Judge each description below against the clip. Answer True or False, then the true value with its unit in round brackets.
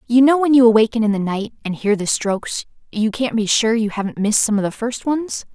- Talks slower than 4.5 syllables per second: False (5.8 syllables/s)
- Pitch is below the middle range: False (225 Hz)